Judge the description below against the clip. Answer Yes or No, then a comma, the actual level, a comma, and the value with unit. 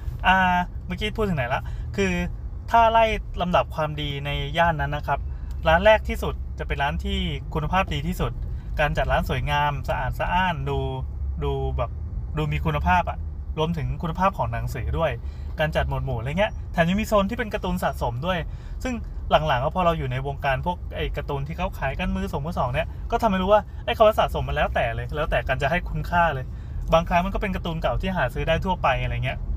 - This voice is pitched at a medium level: Yes, medium, 145 Hz